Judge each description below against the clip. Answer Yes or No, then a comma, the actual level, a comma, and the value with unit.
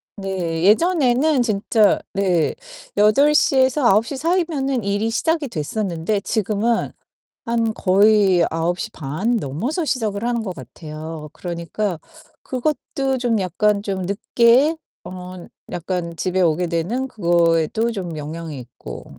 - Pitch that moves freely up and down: Yes, wide, 5.9 semitones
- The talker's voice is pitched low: No, high, 200 Hz